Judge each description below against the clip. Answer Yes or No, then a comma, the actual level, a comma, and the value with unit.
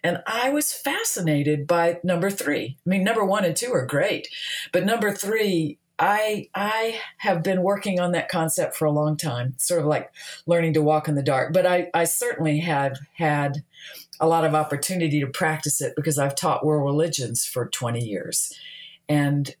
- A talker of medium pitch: Yes, medium, 160 Hz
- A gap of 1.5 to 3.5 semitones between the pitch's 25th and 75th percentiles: No, average, 4.2 semitones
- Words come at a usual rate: Yes, average, 185 wpm